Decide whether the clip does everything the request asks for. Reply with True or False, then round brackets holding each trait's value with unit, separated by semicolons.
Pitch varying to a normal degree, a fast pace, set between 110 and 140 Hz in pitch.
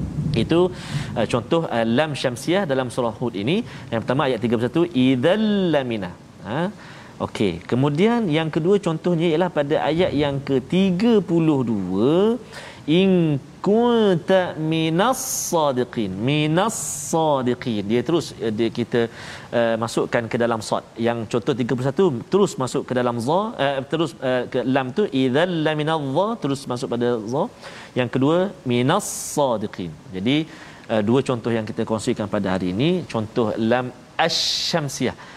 False (5.7 semitones; 135 wpm; 135 Hz)